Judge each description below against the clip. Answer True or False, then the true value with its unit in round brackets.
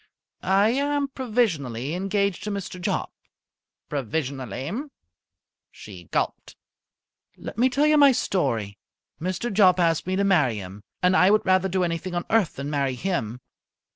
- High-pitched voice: False (180 Hz)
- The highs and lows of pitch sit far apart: True (7.2 semitones)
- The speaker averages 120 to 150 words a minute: True (145 wpm)